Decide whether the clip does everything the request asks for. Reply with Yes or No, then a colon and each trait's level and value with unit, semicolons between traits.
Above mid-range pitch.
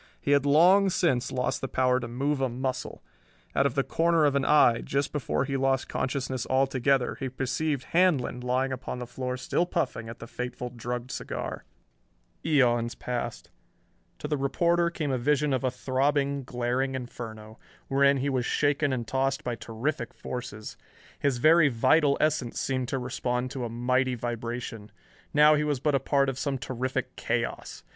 No: low, 130 Hz